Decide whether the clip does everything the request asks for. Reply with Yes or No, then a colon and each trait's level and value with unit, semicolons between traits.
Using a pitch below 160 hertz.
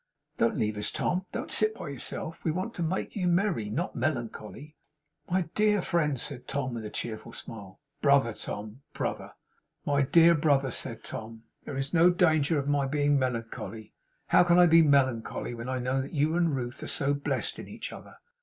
Yes: medium, 140 Hz